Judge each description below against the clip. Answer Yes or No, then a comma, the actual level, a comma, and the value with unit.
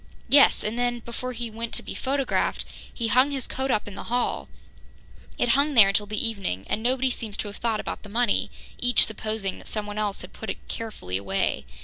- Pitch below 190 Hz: No, high, 225 Hz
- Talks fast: Yes, fast, 215 wpm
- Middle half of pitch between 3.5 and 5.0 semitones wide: No, average, 3.0 semitones